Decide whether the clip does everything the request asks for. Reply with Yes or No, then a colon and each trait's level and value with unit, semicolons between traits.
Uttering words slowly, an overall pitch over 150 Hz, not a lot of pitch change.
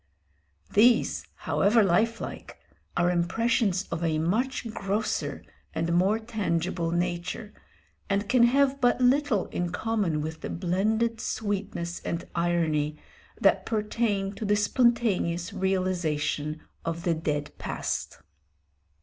No: slow, 115 wpm; high, 190 Hz; average, 4.8 semitones